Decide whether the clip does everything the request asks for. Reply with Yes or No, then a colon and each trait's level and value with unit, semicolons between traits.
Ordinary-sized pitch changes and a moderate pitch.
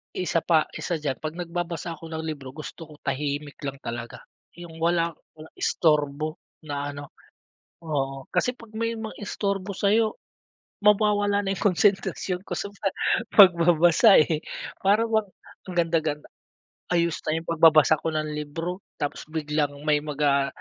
Yes: average, 4.1 semitones; medium, 165 Hz